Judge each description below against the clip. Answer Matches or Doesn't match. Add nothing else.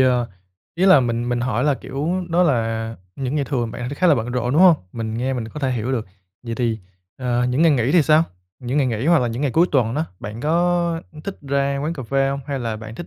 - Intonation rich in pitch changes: Doesn't match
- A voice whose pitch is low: Matches